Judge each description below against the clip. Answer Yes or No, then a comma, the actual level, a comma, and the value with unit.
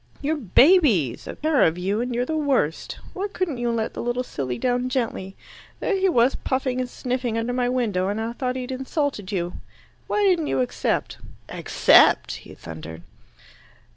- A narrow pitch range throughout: No, average, 5.3 semitones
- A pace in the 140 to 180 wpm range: Yes, average, 175 wpm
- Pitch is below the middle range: No, high, 245 Hz